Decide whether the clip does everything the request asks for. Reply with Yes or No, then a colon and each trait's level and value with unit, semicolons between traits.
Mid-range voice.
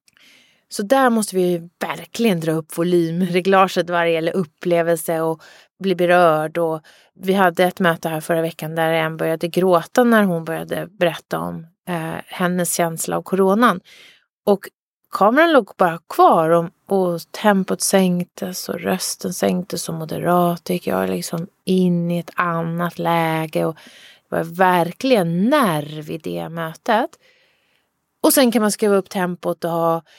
Yes: medium, 175 Hz